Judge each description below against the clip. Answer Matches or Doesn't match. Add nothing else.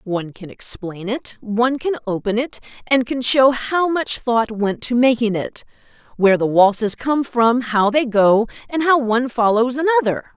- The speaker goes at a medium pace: Matches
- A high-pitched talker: Matches